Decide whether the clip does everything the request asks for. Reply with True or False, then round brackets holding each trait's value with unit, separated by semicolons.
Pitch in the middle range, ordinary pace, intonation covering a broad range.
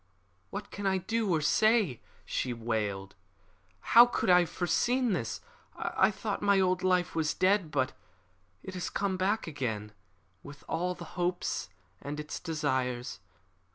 True (175 Hz; 150 wpm; 6.5 semitones)